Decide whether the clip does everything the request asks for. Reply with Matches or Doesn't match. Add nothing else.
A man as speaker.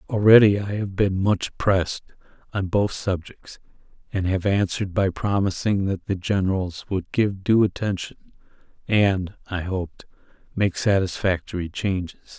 Matches